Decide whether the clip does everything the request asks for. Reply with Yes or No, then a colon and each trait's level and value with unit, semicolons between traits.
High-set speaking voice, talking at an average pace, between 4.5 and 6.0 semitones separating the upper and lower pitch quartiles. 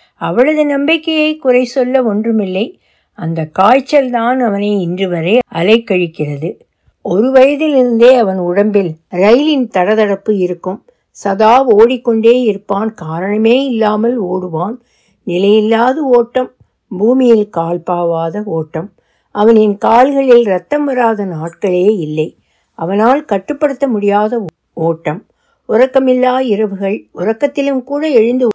Yes: high, 220 Hz; average, 95 wpm; average, 5.2 semitones